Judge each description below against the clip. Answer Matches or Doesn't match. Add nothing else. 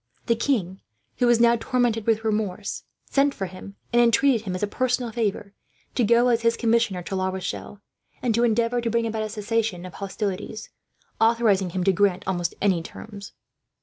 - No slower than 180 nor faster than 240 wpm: Matches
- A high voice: Matches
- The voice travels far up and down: Doesn't match